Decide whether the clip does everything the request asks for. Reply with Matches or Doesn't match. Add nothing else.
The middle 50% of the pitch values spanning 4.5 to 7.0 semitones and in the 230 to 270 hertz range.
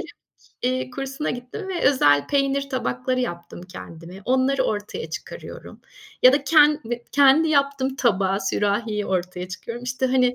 Matches